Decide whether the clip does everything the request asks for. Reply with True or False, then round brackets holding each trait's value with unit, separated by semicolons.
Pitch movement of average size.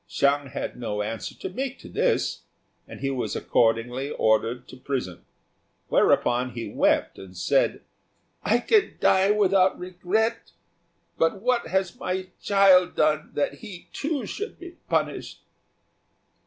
False (8.7 semitones)